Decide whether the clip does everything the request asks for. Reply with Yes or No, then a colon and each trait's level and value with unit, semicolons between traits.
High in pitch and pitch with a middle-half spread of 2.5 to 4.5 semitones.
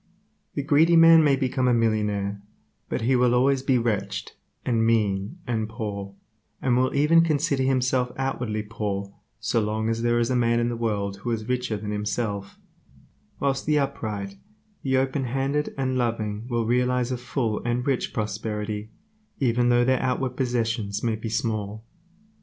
No: low, 120 Hz; average, 3.3 semitones